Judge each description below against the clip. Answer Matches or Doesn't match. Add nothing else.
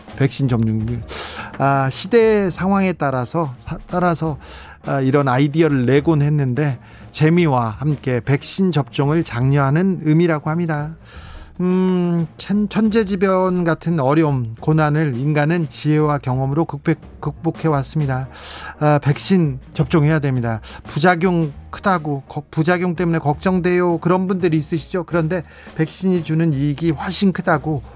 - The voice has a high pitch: Doesn't match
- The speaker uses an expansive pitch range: Doesn't match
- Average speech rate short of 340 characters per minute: Matches